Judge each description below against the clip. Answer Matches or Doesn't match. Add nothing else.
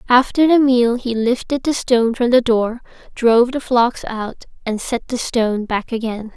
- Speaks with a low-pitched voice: Doesn't match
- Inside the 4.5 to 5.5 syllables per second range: Matches